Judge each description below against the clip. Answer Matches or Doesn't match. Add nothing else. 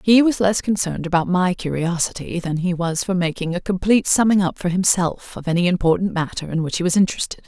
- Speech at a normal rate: Doesn't match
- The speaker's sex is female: Matches